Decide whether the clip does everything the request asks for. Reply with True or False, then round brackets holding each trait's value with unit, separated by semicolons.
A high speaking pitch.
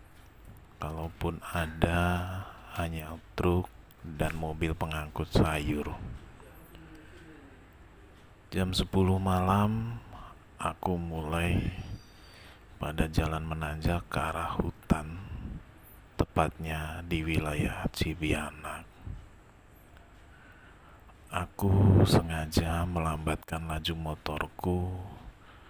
False (85 Hz)